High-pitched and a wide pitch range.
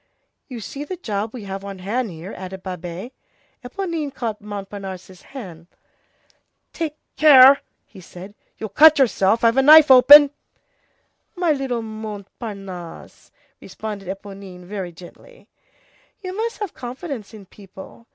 Yes: high, 215 Hz; wide, 6.0 semitones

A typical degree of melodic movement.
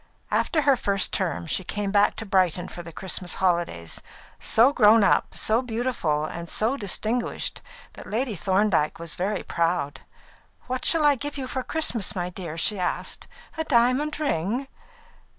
No: wide, 6.2 semitones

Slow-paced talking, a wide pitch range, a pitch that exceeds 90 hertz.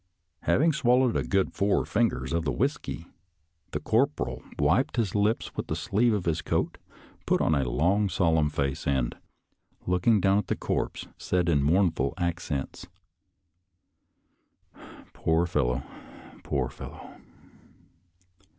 No: slow, 130 wpm; wide, 6.2 semitones; very low, 85 Hz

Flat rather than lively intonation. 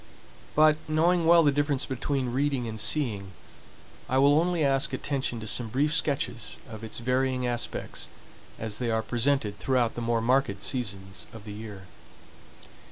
No: average, 4.2 semitones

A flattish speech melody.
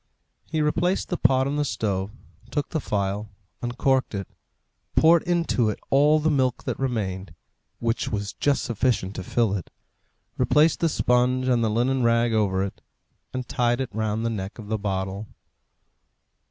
No: average, 4.6 semitones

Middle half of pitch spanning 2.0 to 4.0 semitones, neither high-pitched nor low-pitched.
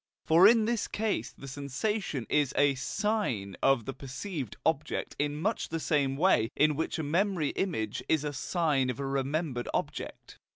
No: average, 4.6 semitones; medium, 145 Hz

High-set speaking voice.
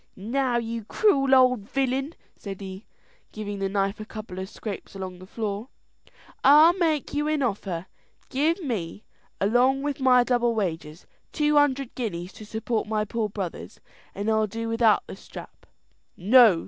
Yes: high, 225 Hz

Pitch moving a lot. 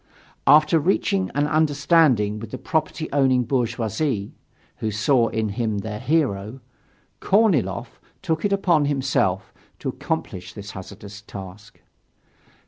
Yes: wide, 6.8 semitones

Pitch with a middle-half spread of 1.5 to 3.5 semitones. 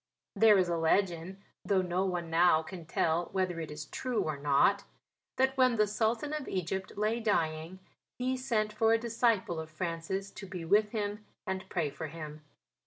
No: average, 4.5 semitones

